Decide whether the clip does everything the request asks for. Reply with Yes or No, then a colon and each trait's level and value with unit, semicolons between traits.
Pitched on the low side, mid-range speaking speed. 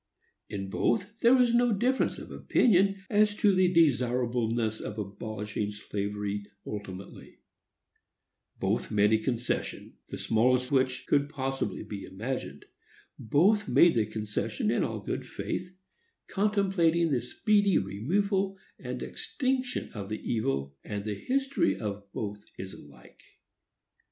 No: low, 125 Hz; slow, 125 wpm